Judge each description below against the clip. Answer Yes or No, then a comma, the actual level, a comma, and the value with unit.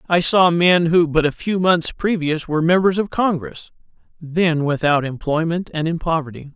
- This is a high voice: No, medium, 165 Hz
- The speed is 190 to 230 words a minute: No, average, 175 wpm